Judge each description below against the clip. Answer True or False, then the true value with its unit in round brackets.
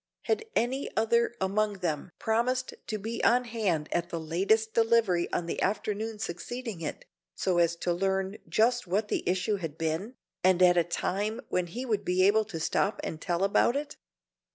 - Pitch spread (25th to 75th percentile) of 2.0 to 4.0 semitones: False (4.4 semitones)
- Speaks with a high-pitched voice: True (200 Hz)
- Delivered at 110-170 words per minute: False (180 wpm)